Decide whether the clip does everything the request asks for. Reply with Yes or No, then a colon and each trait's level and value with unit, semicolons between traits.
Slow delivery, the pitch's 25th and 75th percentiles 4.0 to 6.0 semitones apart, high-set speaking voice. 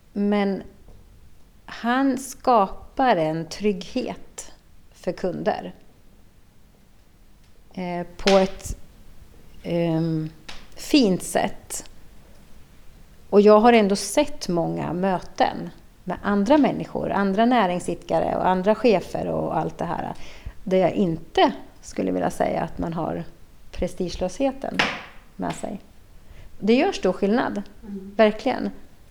Yes: slow, 100 wpm; average, 5.2 semitones; high, 195 Hz